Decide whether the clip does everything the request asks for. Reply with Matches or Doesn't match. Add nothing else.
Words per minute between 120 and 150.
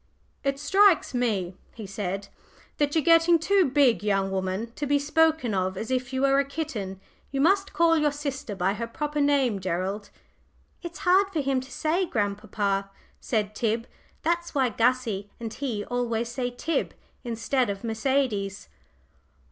Doesn't match